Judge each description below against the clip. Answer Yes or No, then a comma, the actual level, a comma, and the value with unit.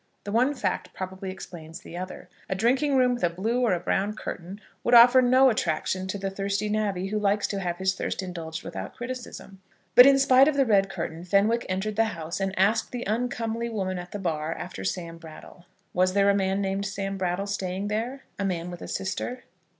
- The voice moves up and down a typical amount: Yes, average, 3.8 semitones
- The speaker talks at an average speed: No, fast, 210 wpm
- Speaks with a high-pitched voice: Yes, high, 195 Hz